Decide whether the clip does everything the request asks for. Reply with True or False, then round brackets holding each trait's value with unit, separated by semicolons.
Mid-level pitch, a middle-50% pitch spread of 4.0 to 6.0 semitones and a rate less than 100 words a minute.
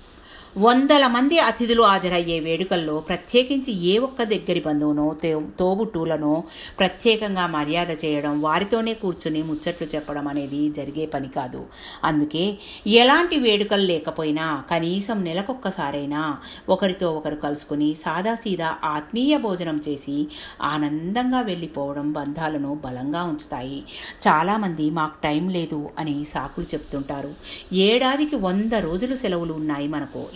False (165 Hz; 5.3 semitones; 105 wpm)